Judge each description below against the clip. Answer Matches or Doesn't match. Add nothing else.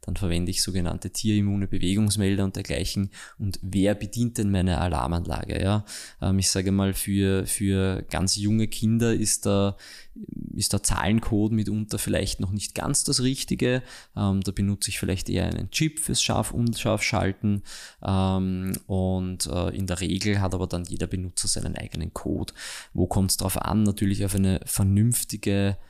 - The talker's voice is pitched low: Matches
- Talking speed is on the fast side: Doesn't match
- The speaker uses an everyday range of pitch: Doesn't match